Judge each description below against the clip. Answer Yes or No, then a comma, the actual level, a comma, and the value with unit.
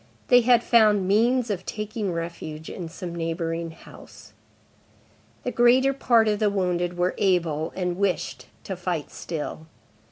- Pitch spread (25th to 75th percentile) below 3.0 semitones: No, average, 4.6 semitones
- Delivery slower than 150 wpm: Yes, average, 140 wpm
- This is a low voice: No, medium, 185 Hz